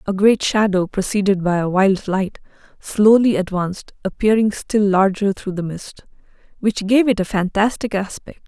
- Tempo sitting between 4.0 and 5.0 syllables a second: Yes, 4.7 syllables/s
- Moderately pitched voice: No, high, 200 Hz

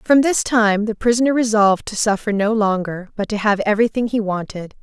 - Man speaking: No, female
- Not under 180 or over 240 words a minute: Yes, average, 200 wpm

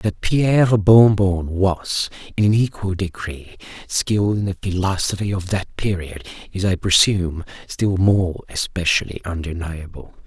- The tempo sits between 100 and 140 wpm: Yes, slow, 135 wpm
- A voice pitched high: No, very low, 95 Hz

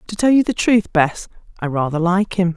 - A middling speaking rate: No, fast, 210 wpm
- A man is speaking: No, female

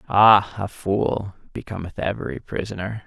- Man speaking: Yes, male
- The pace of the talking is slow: Yes, slow, 115 wpm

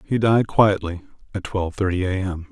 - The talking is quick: No, average, 190 wpm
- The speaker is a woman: No, male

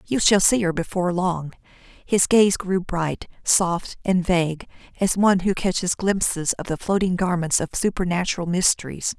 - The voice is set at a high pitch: No, medium, 180 Hz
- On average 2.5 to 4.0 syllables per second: No, 4.7 syllables/s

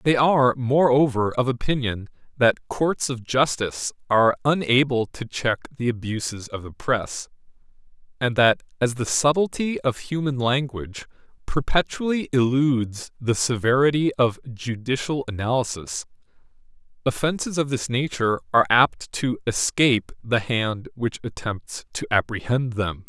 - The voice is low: Yes, low, 125 Hz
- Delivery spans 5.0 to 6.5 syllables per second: No, 4.6 syllables/s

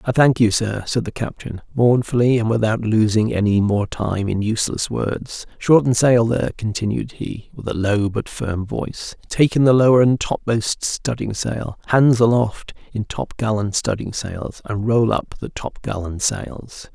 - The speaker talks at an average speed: Yes, average, 170 wpm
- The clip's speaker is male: Yes, male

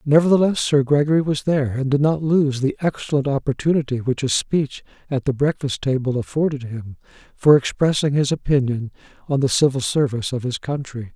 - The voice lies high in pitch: No, medium, 140 Hz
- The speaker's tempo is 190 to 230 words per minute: No, average, 170 wpm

